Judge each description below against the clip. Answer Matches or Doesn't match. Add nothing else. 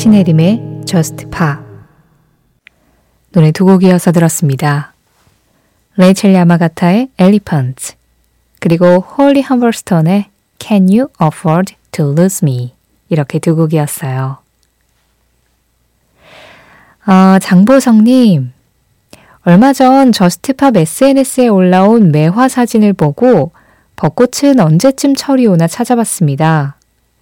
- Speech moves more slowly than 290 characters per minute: Matches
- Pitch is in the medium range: Matches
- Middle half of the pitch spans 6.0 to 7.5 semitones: Matches